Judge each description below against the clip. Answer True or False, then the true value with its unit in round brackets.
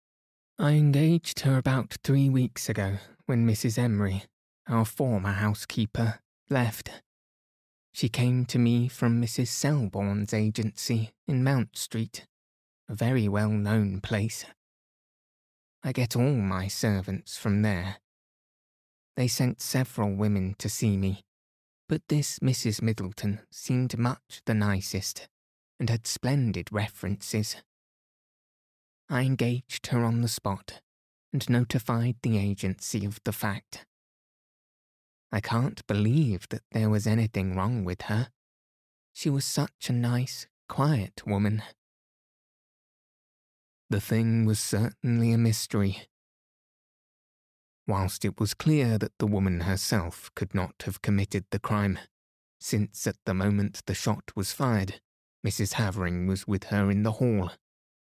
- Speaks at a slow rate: True (125 wpm)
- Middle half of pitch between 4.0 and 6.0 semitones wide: False (3.4 semitones)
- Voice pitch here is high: False (110 Hz)